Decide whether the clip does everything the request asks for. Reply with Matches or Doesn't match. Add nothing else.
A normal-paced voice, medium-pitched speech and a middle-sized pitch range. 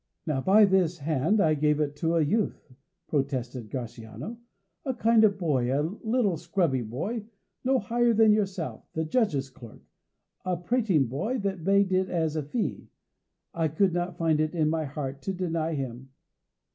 Doesn't match